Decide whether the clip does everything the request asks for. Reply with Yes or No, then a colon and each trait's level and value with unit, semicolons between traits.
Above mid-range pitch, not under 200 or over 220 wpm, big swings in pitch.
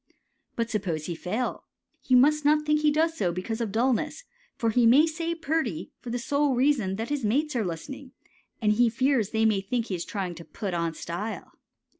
Yes: high, 235 Hz; fast, 205 wpm; wide, 6.4 semitones